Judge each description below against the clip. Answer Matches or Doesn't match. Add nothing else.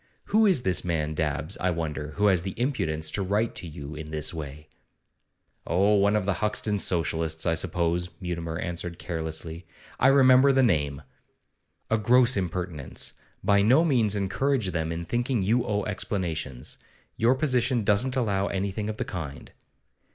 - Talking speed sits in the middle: Matches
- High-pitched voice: Doesn't match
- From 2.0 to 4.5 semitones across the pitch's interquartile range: Doesn't match